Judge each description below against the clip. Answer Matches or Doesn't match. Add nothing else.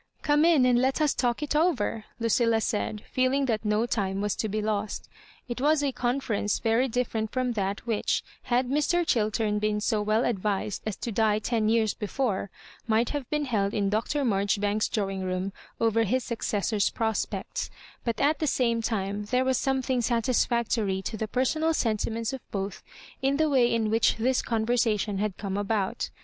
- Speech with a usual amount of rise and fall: Matches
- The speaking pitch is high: Matches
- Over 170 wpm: Matches